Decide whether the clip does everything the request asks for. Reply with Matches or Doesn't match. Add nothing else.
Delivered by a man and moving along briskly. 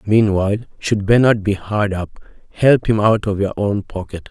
Doesn't match